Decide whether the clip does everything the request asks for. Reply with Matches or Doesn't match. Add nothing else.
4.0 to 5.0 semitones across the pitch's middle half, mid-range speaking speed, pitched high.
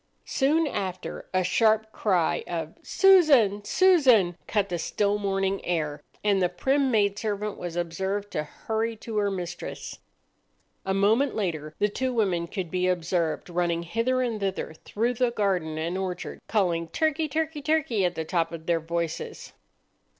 Matches